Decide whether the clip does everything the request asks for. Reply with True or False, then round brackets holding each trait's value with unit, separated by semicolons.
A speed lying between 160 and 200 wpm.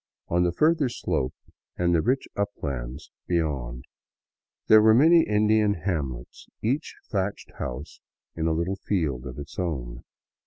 False (145 wpm)